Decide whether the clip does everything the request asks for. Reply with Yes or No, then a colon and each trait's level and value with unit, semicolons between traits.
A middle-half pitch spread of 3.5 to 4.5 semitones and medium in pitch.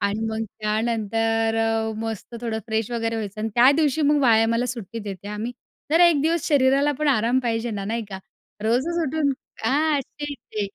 No: average, 4.1 semitones; high, 230 Hz